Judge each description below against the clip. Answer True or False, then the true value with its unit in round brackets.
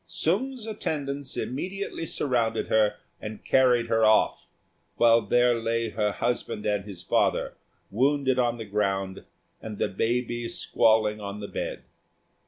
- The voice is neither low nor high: False (115 Hz)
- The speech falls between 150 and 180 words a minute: False (135 wpm)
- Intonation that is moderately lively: True (3.6 semitones)